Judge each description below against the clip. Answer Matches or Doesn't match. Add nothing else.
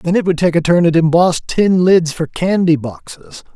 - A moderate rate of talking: Doesn't match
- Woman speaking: Doesn't match